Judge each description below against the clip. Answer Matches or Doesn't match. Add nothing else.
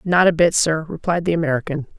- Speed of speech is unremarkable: Doesn't match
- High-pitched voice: Doesn't match